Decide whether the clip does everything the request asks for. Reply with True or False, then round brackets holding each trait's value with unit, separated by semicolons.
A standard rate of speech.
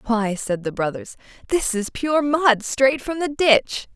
True (180 wpm)